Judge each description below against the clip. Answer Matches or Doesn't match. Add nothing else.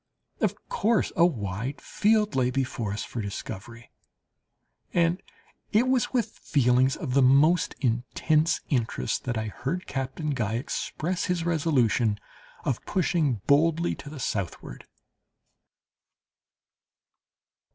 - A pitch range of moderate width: Doesn't match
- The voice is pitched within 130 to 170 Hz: Matches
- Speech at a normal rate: Doesn't match